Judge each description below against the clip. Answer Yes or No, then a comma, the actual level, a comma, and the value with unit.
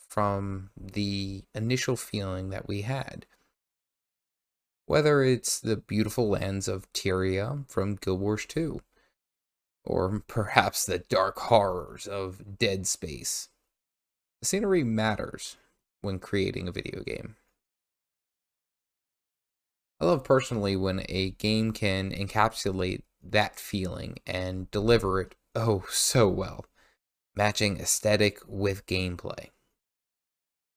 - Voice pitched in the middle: No, low, 100 Hz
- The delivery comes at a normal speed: No, slow, 105 wpm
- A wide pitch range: No, narrow, 2.5 semitones